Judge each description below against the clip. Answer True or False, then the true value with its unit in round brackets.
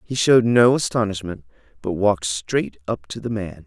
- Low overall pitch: True (105 Hz)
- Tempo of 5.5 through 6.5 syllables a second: False (5.2 syllables/s)